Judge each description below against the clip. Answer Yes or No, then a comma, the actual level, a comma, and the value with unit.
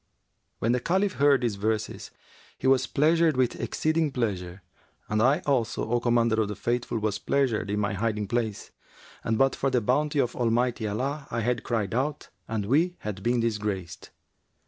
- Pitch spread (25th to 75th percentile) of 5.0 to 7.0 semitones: No, average, 4.0 semitones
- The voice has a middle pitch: No, low, 120 Hz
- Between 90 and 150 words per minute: No, average, 175 wpm